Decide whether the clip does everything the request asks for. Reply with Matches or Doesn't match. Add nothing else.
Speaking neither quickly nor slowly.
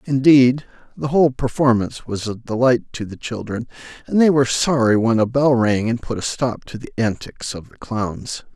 Matches